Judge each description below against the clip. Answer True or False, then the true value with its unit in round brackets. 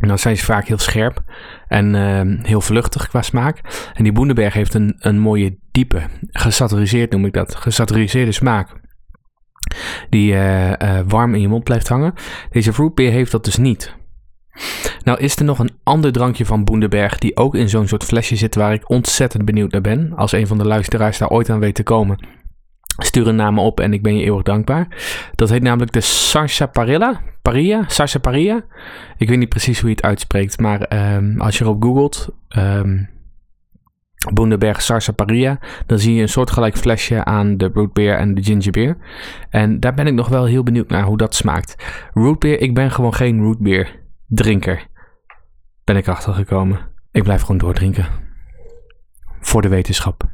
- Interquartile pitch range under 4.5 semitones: True (3.1 semitones)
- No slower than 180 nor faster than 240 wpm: True (185 wpm)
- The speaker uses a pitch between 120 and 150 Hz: False (110 Hz)